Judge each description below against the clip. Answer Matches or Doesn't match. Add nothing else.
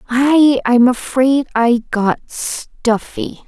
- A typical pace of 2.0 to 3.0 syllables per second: Matches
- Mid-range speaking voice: Doesn't match